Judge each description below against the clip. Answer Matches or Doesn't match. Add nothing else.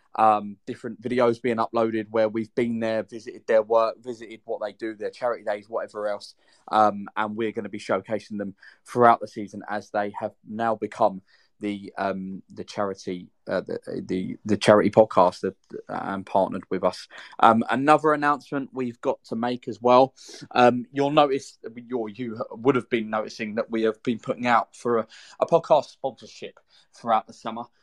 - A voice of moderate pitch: Doesn't match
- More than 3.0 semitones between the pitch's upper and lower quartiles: Doesn't match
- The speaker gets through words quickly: Doesn't match